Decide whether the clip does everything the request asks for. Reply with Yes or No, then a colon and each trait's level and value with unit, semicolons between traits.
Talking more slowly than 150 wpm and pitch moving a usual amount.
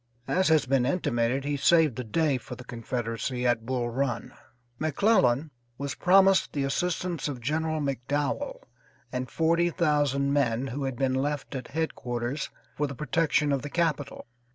No: average, 155 wpm; average, 4.0 semitones